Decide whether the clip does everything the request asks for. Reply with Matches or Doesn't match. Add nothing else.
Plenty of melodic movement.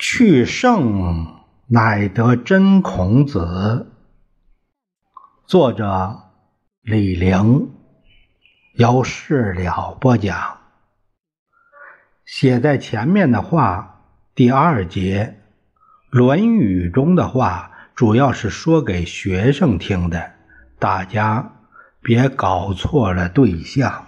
Matches